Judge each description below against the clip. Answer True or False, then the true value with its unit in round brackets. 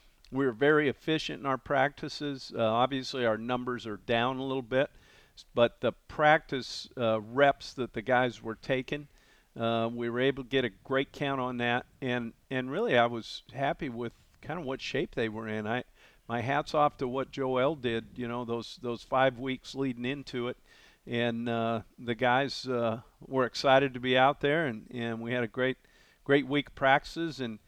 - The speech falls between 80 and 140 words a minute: False (195 wpm)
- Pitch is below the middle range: True (125 Hz)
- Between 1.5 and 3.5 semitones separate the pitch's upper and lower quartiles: True (2.5 semitones)